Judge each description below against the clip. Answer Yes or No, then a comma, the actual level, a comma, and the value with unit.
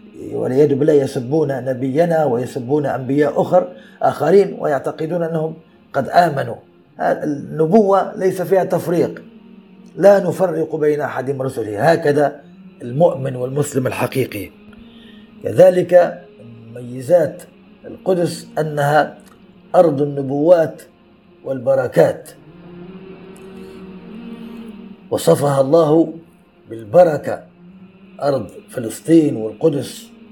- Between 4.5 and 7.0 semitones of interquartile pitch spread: Yes, average, 4.9 semitones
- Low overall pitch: No, medium, 165 Hz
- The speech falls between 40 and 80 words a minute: Yes, average, 75 wpm